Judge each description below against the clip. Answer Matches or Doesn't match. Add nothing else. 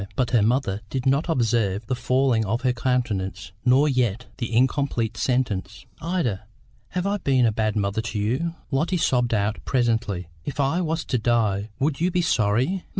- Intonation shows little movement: Doesn't match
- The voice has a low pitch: Matches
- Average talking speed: Matches